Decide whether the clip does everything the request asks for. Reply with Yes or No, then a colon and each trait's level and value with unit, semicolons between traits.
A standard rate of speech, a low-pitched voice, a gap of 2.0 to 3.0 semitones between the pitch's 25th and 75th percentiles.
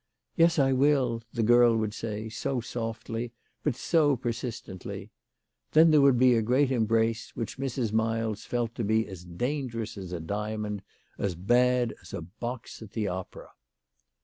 Yes: average, 170 wpm; low, 115 Hz; average, 2.7 semitones